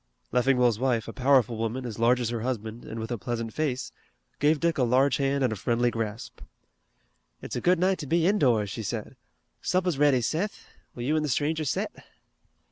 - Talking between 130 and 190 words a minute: No, average, 200 wpm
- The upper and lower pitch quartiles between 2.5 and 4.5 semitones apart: Yes, average, 4.2 semitones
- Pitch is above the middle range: No, low, 125 Hz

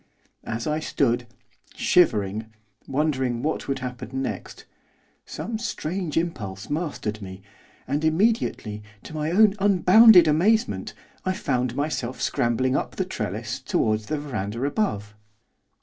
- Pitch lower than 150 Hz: Yes, medium, 140 Hz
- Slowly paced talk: Yes, slow, 120 wpm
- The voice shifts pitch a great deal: Yes, wide, 6.8 semitones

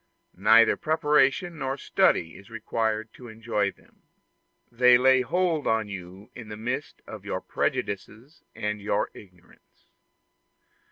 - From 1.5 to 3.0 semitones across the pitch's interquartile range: No, average, 4.2 semitones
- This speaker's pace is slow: Yes, slow, 125 wpm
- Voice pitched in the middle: No, low, 115 Hz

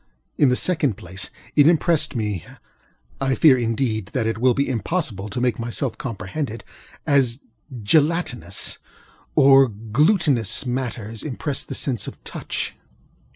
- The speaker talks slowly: Yes, slow, 130 wpm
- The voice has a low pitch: Yes, low, 125 Hz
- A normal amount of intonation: Yes, average, 4.5 semitones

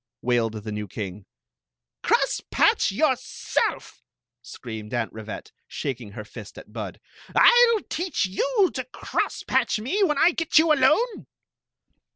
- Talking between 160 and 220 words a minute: No, average, 140 wpm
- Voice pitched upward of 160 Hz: Yes, medium, 185 Hz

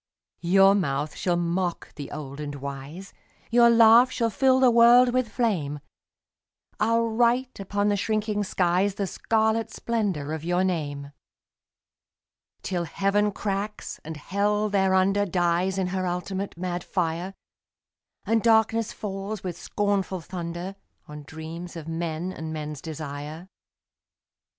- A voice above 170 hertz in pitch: Yes, high, 190 Hz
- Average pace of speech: No, slow, 130 wpm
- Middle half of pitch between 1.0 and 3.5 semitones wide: No, average, 4.3 semitones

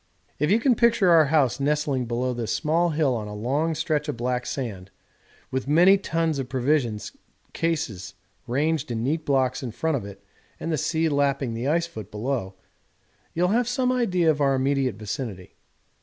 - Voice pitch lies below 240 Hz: Yes, medium, 140 Hz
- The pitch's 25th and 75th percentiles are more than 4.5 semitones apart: Yes, average, 5.0 semitones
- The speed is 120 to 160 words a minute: No, average, 180 wpm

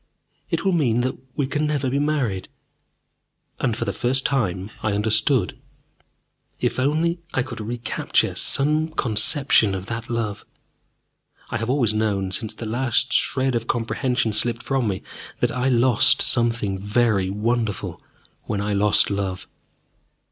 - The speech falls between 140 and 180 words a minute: Yes, average, 150 wpm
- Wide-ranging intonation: No, average, 4.0 semitones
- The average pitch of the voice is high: No, low, 115 Hz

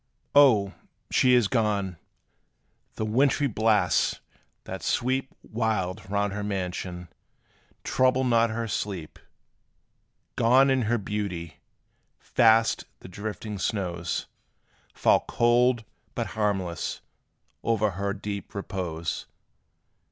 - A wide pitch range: No, average, 3.4 semitones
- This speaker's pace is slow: Yes, slow, 100 wpm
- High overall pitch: No, low, 105 Hz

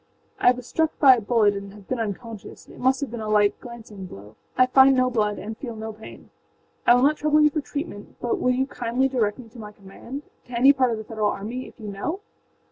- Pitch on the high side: Yes, high, 235 Hz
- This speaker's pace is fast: Yes, fast, 235 wpm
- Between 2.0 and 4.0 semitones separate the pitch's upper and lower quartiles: Yes, average, 3.7 semitones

